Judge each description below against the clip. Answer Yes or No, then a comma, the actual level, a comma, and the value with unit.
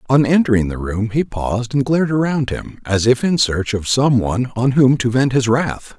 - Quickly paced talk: Yes, fast, 230 wpm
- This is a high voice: No, low, 125 Hz